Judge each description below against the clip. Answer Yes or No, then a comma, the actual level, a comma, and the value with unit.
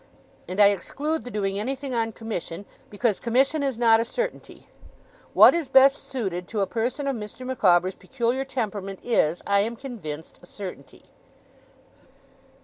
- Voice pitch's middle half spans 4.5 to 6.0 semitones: Yes, average, 5.0 semitones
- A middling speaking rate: Yes, average, 150 wpm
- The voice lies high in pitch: Yes, high, 225 Hz